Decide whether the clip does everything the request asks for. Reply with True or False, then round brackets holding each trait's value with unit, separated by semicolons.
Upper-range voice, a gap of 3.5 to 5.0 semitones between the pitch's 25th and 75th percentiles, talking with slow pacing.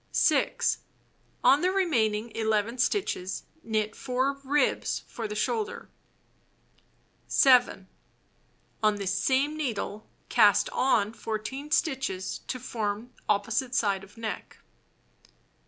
True (225 Hz; 4.2 semitones; 105 wpm)